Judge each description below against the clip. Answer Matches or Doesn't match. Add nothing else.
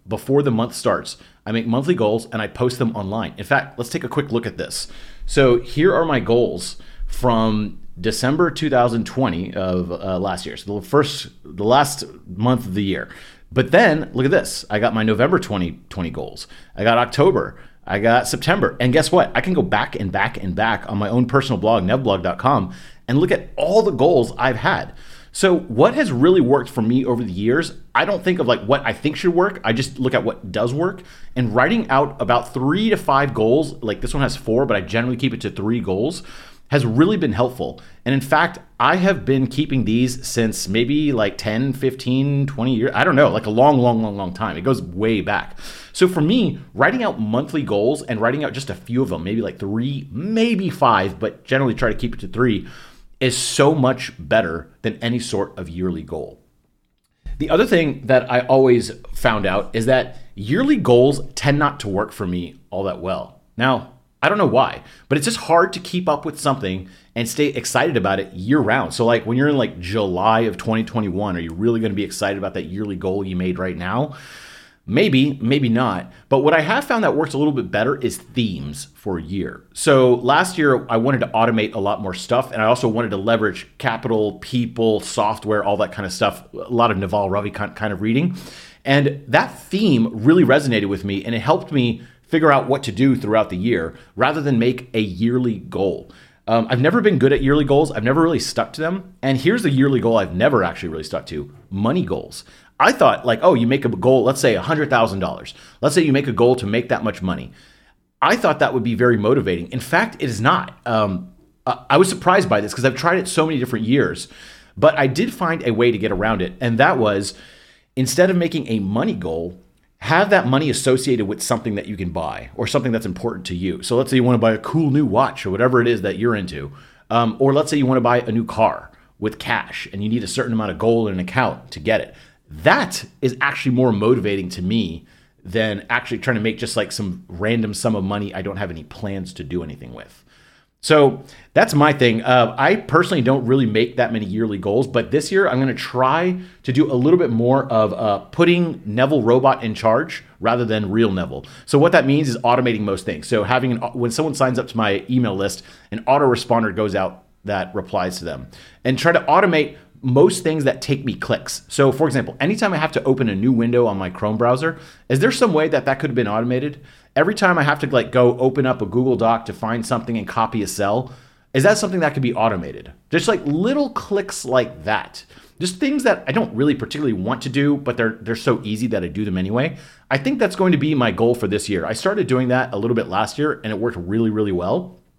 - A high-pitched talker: Doesn't match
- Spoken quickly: Matches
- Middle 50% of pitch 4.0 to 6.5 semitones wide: Matches